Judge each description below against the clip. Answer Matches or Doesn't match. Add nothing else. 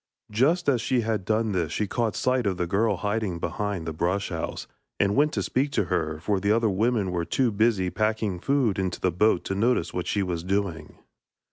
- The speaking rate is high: Matches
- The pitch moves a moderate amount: Matches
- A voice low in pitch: Matches